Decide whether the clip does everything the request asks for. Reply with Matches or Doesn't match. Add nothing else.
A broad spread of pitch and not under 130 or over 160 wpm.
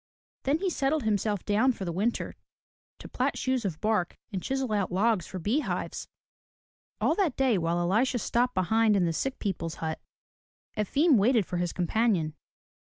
Doesn't match